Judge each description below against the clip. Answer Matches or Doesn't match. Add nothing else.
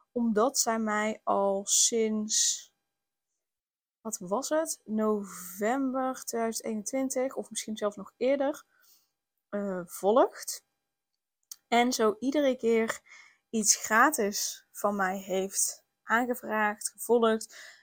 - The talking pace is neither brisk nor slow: Doesn't match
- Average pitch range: Matches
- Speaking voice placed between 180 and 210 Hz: Doesn't match